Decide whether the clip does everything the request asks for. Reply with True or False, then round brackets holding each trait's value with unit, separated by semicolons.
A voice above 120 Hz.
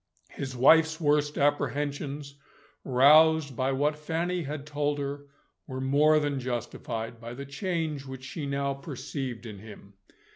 True (140 Hz)